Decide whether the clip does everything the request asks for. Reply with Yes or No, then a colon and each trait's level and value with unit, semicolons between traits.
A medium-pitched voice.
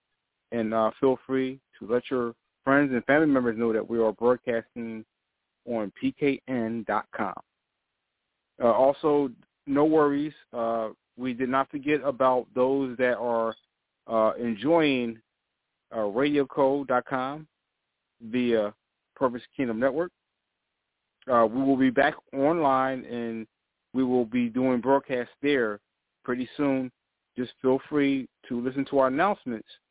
No: low, 130 Hz